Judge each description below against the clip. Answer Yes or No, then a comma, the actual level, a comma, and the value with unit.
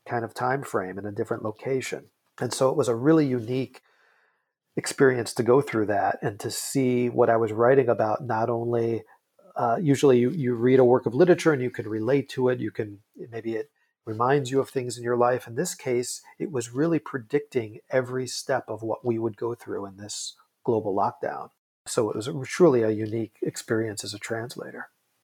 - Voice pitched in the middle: No, low, 120 Hz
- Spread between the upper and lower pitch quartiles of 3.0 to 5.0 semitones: No, narrow, 2.6 semitones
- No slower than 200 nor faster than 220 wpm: Yes, fast, 205 wpm